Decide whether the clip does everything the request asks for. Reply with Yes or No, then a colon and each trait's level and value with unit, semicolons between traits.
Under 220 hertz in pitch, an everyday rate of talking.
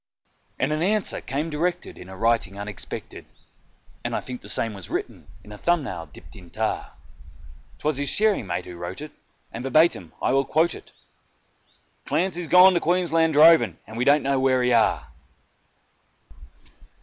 Yes: low, 135 Hz; average, 170 wpm